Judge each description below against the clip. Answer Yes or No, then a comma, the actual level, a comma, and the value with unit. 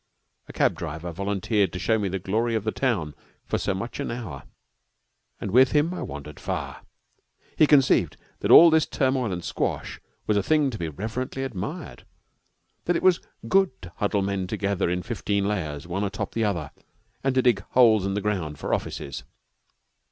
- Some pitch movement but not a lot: No, wide, 5.7 semitones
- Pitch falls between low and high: No, low, 105 Hz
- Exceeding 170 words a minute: Yes, average, 190 wpm